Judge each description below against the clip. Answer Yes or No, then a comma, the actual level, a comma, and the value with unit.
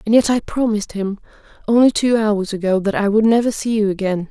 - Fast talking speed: Yes, fast, 225 wpm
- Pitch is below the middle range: No, high, 215 Hz